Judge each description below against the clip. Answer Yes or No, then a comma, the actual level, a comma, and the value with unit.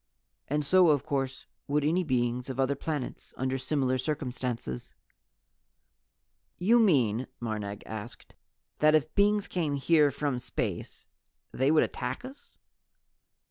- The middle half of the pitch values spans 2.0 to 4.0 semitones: Yes, average, 3.7 semitones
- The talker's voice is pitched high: No, medium, 140 Hz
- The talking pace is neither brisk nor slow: No, slow, 125 wpm